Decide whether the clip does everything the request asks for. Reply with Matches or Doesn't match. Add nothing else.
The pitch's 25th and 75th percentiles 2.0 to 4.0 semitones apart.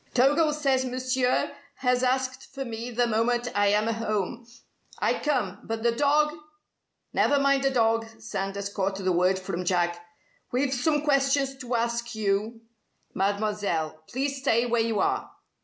Doesn't match